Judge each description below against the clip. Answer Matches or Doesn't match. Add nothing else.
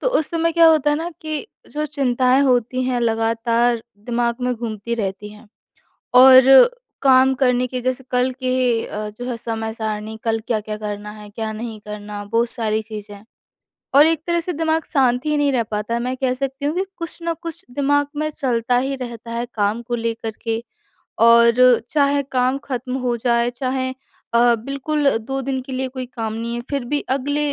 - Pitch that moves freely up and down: Doesn't match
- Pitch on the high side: Matches